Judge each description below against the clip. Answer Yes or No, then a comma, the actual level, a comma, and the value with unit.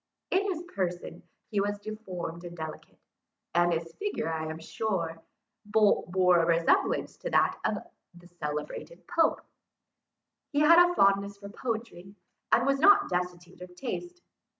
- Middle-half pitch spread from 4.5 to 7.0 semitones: Yes, wide, 5.4 semitones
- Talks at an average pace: Yes, average, 145 wpm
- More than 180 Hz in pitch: Yes, high, 190 Hz